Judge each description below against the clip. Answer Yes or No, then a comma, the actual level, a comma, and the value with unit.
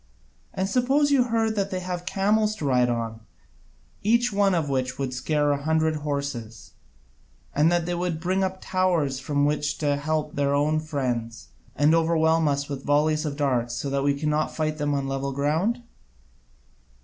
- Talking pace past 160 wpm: Yes, average, 175 wpm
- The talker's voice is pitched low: No, medium, 150 Hz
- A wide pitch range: No, average, 4.4 semitones